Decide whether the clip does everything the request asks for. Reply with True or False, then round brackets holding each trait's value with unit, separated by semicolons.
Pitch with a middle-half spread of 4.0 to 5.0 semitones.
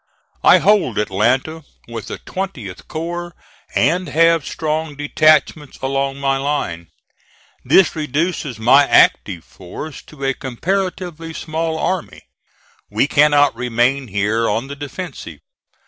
True (4.7 semitones)